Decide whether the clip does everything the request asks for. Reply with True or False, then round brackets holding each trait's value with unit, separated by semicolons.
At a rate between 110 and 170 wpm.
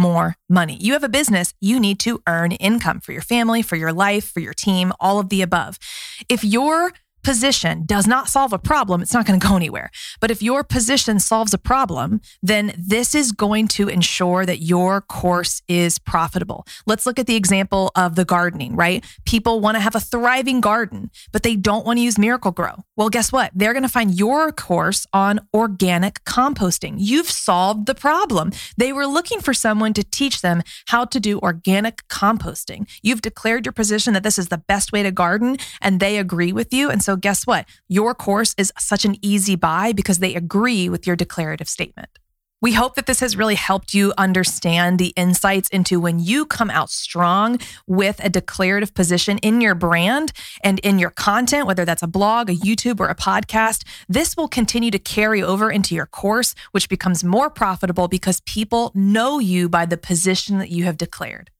False (200 wpm)